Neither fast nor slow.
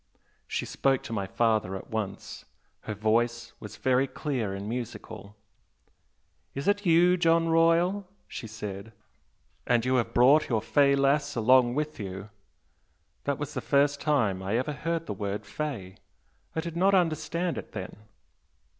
Yes: average, 155 wpm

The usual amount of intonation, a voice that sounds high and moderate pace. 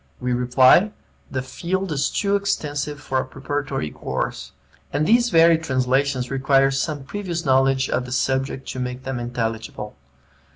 No: average, 3.3 semitones; low, 135 Hz; average, 150 wpm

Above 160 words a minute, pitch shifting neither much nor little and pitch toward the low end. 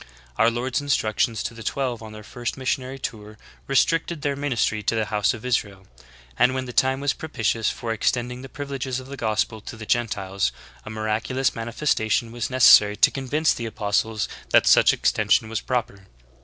Yes: average, 185 wpm; average, 3.4 semitones; low, 120 Hz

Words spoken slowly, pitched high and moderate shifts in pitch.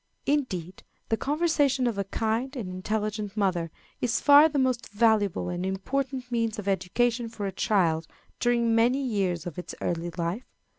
No: average, 160 wpm; high, 220 Hz; average, 4.7 semitones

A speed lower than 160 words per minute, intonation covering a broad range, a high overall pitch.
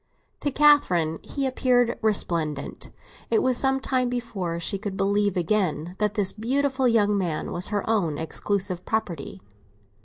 Yes: average, 145 wpm; wide, 5.9 semitones; high, 205 Hz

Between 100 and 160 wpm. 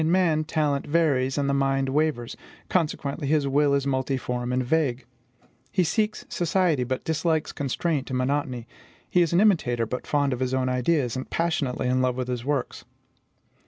No: average, 175 wpm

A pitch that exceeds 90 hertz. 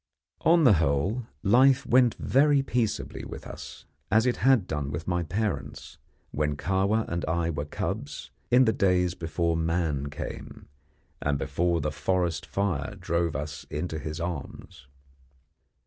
No: very low, 85 Hz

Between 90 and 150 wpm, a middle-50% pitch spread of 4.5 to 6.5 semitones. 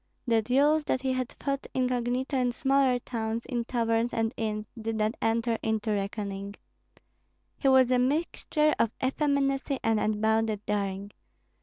No: average, 145 wpm; average, 3.2 semitones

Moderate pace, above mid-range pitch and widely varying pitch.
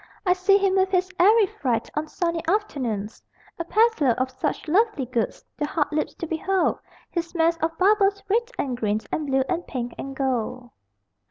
Yes: average, 180 wpm; very high, 330 Hz; wide, 6.5 semitones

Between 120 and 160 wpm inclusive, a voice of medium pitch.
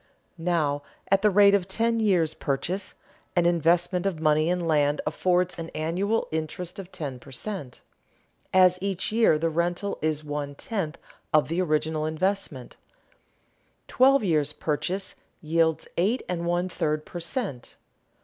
Yes: average, 145 wpm; medium, 170 Hz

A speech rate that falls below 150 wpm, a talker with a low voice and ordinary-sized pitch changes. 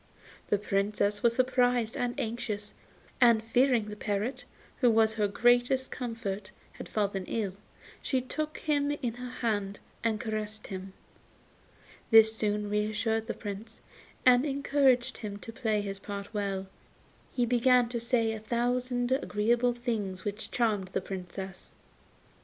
No: average, 140 wpm; high, 225 Hz; average, 3.0 semitones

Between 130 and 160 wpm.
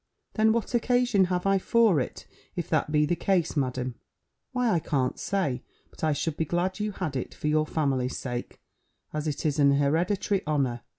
No: average, 190 wpm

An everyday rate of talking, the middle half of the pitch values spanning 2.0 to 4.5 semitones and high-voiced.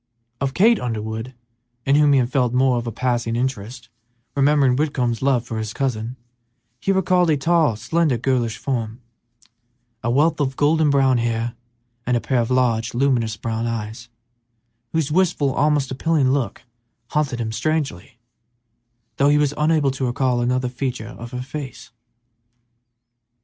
No: average, 150 wpm; average, 3.5 semitones; low, 130 Hz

